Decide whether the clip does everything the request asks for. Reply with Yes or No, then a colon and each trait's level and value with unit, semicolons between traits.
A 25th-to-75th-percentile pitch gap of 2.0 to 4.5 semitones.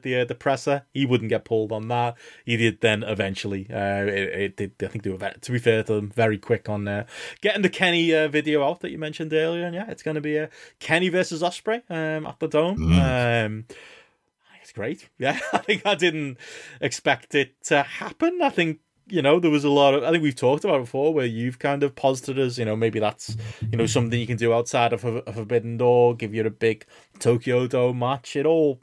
No: wide, 5.4 semitones